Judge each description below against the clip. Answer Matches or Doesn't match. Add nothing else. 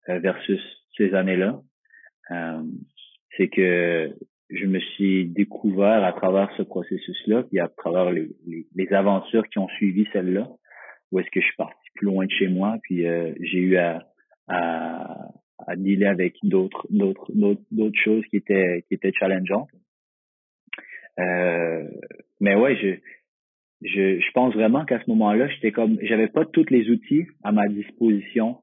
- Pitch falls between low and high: Doesn't match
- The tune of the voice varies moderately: Matches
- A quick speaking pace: Doesn't match